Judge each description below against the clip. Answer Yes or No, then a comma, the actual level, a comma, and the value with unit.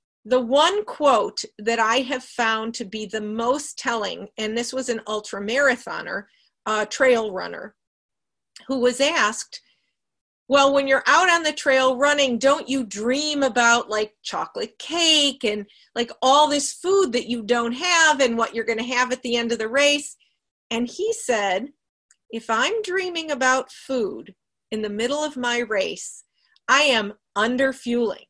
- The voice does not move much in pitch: No, average, 3.8 semitones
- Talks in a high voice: Yes, very high, 255 Hz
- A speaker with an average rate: Yes, average, 160 wpm